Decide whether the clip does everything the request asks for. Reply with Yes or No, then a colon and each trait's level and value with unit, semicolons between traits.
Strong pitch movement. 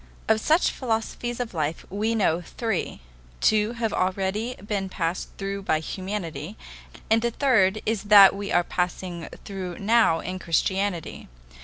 No: average, 3.3 semitones